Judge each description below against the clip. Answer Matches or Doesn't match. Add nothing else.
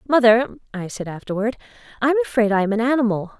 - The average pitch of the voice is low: Doesn't match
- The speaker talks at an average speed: Matches